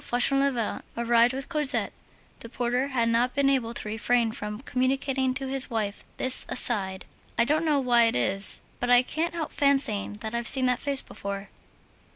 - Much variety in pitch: No, average, 3.0 semitones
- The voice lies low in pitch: No, high, 245 Hz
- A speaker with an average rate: Yes, average, 180 wpm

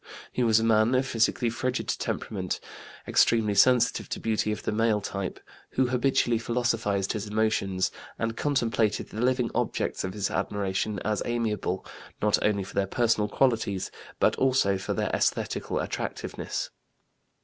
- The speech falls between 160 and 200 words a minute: No, average, 150 wpm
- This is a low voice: Yes, low, 110 Hz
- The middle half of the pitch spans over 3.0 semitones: No, average, 2.7 semitones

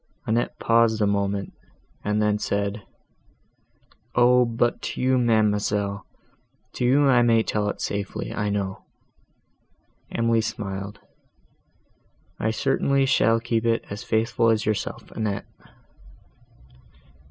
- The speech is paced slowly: Yes, slow, 115 wpm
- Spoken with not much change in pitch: Yes, narrow, 2.3 semitones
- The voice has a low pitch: Yes, low, 110 Hz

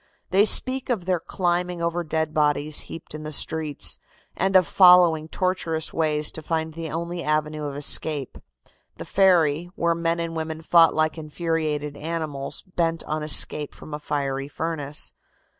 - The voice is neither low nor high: Yes, medium, 160 Hz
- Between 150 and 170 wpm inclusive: Yes, average, 160 wpm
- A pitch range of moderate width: No, narrow, 2.0 semitones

